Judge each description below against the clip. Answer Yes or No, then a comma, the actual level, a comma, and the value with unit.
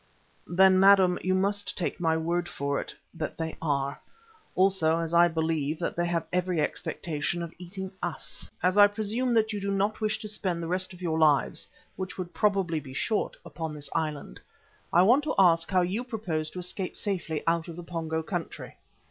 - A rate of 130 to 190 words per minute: No, average, 200 wpm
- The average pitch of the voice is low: No, medium, 175 Hz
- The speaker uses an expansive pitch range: No, average, 3.2 semitones